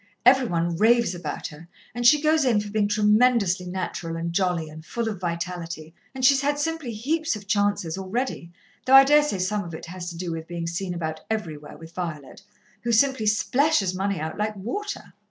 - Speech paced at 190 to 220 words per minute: Yes, average, 195 wpm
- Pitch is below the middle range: No, high, 200 Hz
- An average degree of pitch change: No, wide, 6.1 semitones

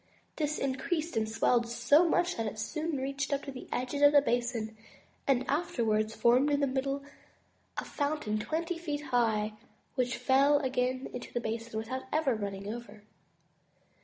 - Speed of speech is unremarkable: Yes, average, 160 wpm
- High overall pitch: Yes, very high, 260 Hz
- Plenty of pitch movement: No, average, 4.0 semitones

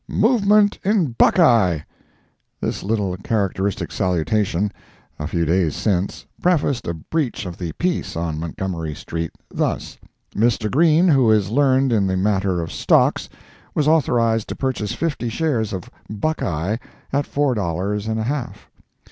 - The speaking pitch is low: Yes, low, 110 Hz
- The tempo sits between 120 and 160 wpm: Yes, average, 140 wpm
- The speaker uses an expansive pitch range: Yes, wide, 7.3 semitones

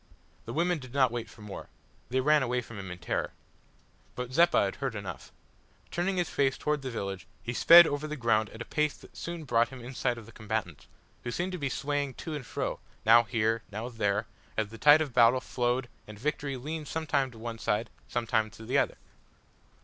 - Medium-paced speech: No, fast, 215 wpm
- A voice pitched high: No, low, 125 Hz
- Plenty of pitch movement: No, average, 4.6 semitones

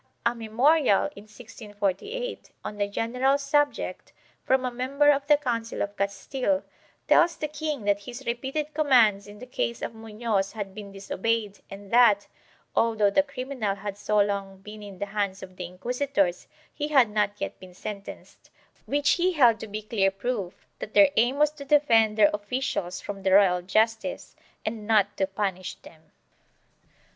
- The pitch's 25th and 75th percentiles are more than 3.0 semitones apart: Yes, average, 4.8 semitones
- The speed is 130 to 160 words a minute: No, average, 170 wpm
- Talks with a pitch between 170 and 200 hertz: No, high, 220 Hz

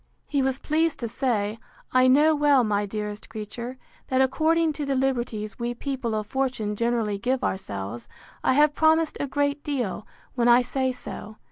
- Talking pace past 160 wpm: Yes, average, 170 wpm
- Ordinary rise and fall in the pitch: Yes, average, 4.6 semitones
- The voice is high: Yes, very high, 255 Hz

